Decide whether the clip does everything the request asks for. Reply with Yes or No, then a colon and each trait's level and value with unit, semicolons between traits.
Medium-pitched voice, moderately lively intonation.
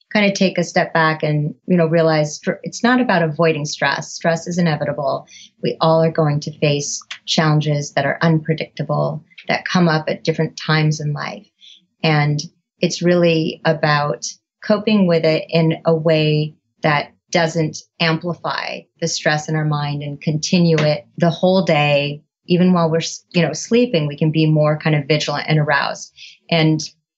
No: medium, 160 Hz; narrow, 1.9 semitones